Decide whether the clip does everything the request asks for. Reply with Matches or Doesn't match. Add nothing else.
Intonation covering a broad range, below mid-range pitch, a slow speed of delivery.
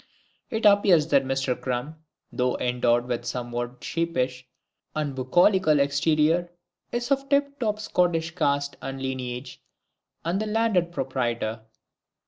Doesn't match